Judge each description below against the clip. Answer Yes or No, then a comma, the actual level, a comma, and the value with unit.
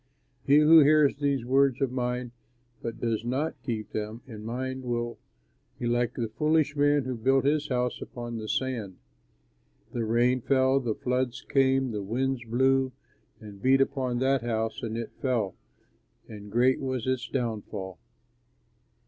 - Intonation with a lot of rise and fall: No, narrow, 2.4 semitones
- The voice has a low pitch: Yes, low, 125 Hz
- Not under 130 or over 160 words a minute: Yes, average, 150 wpm